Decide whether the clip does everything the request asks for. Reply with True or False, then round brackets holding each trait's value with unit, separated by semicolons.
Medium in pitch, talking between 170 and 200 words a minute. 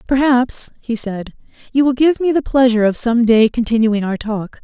False (240 Hz; 195 wpm)